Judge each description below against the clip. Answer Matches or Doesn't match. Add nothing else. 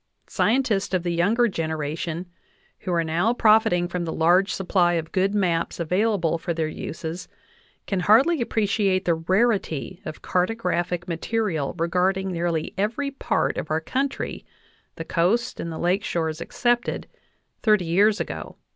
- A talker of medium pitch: Matches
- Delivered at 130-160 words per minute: Matches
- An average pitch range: Matches